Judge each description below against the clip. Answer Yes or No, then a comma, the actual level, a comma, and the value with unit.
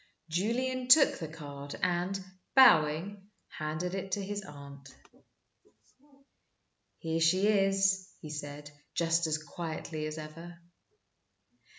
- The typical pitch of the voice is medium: Yes, medium, 170 Hz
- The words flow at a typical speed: No, slow, 105 wpm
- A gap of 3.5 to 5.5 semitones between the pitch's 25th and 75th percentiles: Yes, average, 4.2 semitones